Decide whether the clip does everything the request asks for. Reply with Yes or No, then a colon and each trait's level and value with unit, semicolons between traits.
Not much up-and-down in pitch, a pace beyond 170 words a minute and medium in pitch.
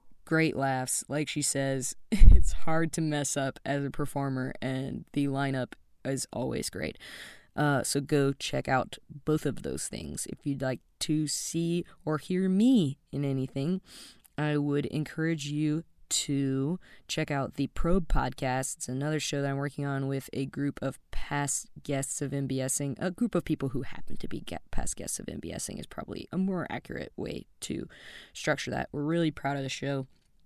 Yes: narrow, 2.3 semitones; average, 180 wpm; medium, 145 Hz